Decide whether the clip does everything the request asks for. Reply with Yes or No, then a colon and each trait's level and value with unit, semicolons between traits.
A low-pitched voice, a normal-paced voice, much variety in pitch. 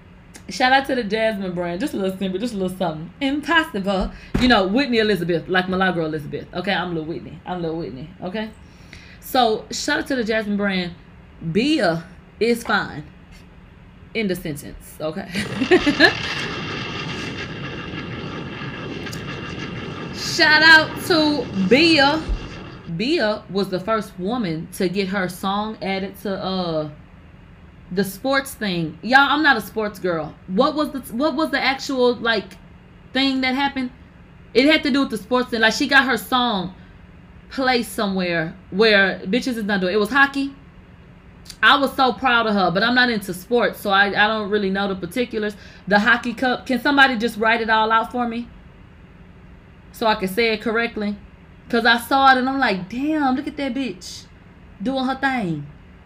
No: high, 220 Hz; average, 165 wpm; wide, 5.7 semitones